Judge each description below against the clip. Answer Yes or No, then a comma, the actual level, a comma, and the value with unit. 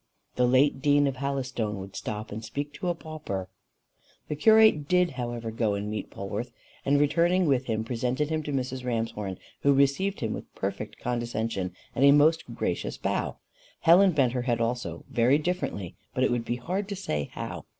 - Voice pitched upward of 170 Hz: No, low, 130 Hz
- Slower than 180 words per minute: No, average, 185 wpm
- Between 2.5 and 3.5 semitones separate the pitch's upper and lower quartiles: No, average, 4.7 semitones